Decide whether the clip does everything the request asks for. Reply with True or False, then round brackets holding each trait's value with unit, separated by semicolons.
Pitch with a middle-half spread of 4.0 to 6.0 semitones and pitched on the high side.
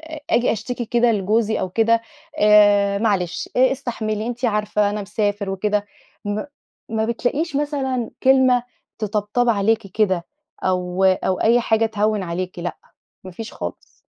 False (3.0 semitones; 215 Hz)